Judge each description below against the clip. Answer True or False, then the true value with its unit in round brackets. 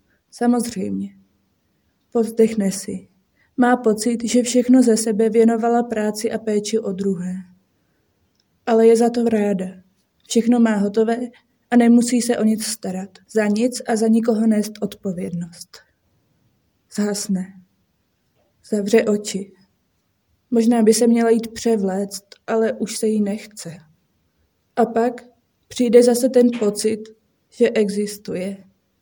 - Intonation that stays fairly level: False (3.5 semitones)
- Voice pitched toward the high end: True (215 Hz)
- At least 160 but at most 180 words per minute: False (120 wpm)